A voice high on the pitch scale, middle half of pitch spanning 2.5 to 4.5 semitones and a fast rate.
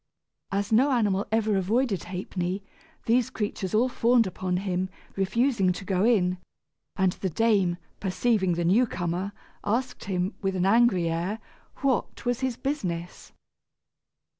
No: high, 195 Hz; average, 4.2 semitones; average, 140 wpm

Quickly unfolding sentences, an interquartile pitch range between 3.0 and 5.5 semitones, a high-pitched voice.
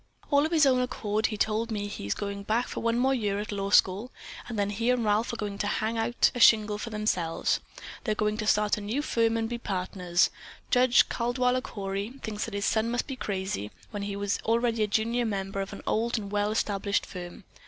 No: fast, 225 wpm; narrow, 2.6 semitones; high, 215 Hz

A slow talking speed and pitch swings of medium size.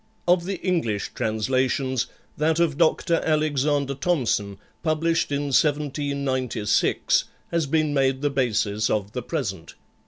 Yes: slow, 120 wpm; average, 3.9 semitones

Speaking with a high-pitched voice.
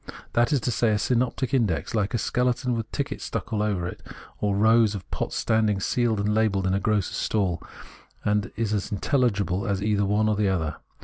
No: low, 105 Hz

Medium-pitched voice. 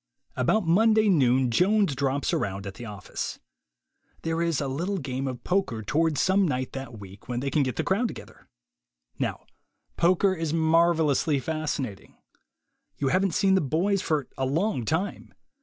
Yes: medium, 155 Hz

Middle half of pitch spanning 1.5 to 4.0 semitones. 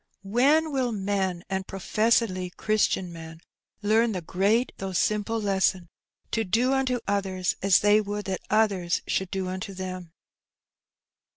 Yes: average, 3.0 semitones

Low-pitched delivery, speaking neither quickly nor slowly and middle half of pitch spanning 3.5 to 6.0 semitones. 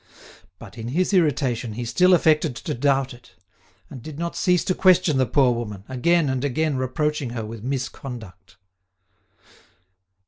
Yes: low, 130 Hz; average, 150 wpm; average, 4.8 semitones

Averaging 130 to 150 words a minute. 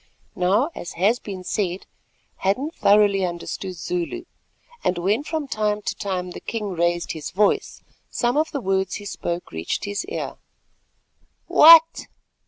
Yes: average, 145 wpm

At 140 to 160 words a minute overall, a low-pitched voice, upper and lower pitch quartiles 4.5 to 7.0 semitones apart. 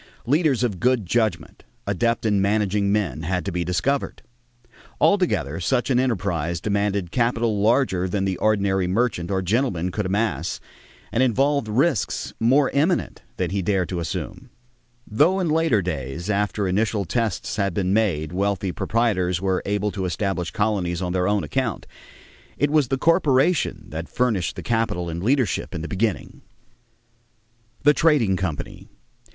Yes: average, 150 wpm; low, 105 Hz; average, 5.0 semitones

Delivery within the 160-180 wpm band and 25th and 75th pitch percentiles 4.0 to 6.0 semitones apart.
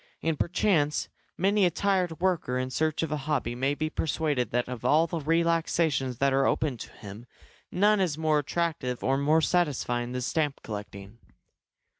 Yes: average, 170 wpm; average, 4.7 semitones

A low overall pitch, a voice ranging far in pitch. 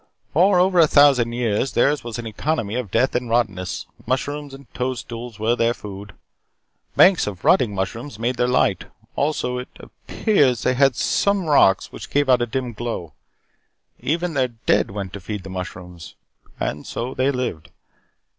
No: low, 120 Hz; average, 4.8 semitones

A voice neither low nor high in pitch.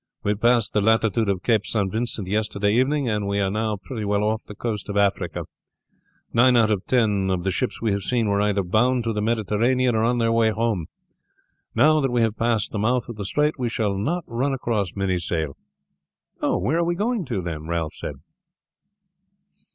No: low, 110 Hz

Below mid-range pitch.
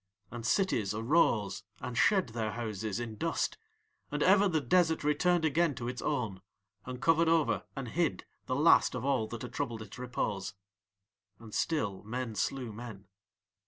Yes: low, 125 Hz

